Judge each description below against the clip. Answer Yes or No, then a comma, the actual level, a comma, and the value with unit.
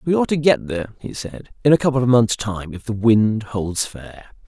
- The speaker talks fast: Yes, fast, 240 wpm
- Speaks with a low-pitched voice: Yes, low, 115 Hz